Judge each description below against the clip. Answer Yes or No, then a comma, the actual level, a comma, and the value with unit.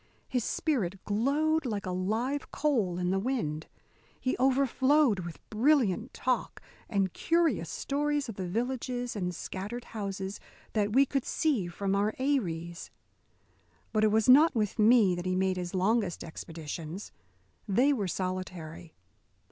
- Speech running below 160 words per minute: Yes, average, 140 wpm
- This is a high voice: Yes, high, 215 Hz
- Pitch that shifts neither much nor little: No, wide, 5.9 semitones